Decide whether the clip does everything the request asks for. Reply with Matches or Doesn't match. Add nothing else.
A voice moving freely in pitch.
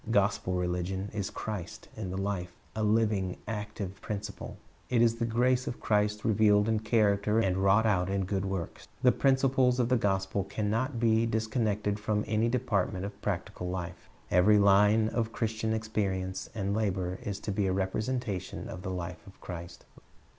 Doesn't match